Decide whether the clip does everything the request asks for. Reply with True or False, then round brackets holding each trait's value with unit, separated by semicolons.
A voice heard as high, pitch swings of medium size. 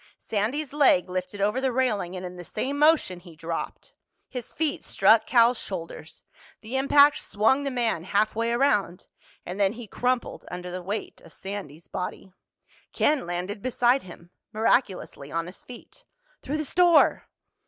False (215 Hz; 6.2 semitones)